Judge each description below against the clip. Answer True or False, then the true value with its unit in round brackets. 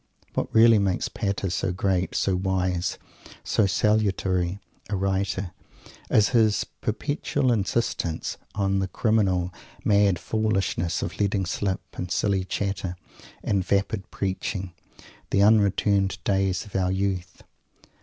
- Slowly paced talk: True (120 wpm)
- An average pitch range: False (1.8 semitones)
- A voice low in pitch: True (95 Hz)